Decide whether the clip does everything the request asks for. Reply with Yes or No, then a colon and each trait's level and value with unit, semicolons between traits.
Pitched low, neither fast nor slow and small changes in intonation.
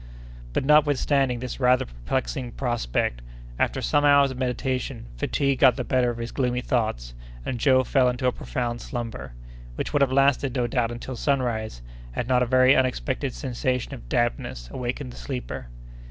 Yes: low, 125 Hz; average, 170 wpm; narrow, 1.9 semitones